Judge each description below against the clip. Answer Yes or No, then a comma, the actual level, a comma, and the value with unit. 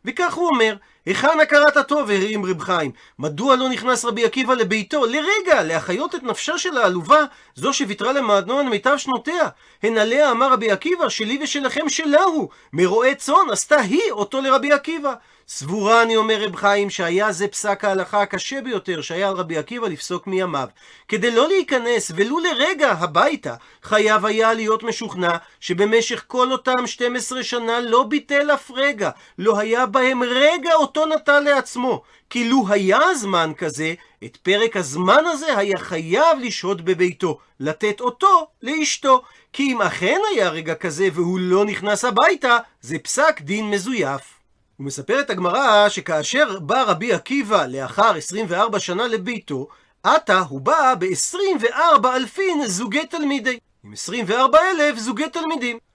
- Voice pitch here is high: Yes, high, 240 Hz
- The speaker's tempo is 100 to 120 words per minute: No, fast, 150 wpm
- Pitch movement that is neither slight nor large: No, wide, 6.3 semitones